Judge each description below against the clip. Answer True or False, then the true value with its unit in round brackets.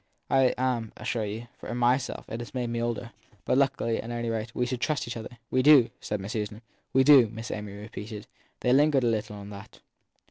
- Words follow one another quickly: True (215 wpm)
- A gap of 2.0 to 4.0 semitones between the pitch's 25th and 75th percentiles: True (2.7 semitones)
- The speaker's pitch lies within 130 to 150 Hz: False (120 Hz)